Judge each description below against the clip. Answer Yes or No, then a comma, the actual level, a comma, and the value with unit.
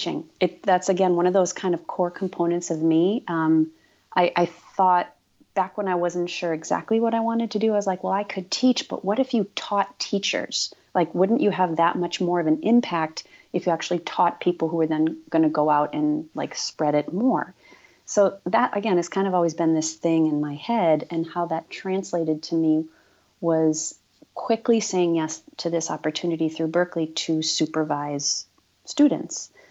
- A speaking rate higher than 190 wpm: Yes, average, 200 wpm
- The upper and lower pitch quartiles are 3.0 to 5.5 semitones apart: Yes, average, 3.4 semitones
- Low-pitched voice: No, medium, 175 Hz